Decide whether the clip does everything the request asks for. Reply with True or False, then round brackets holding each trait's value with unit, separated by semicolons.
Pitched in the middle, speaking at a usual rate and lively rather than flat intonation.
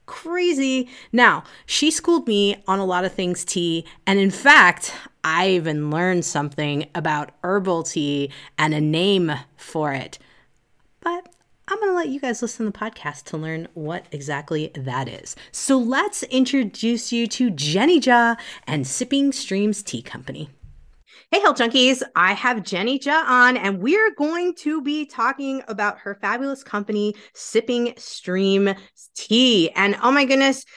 False (210 Hz; 160 wpm; 7.4 semitones)